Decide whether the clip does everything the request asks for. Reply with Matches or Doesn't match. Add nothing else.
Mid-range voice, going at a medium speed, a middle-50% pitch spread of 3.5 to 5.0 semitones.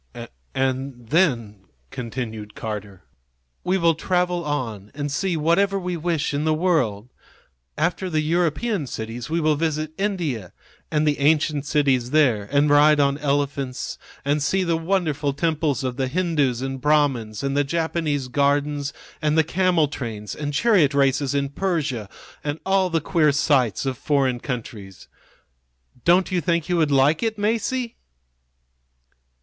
Matches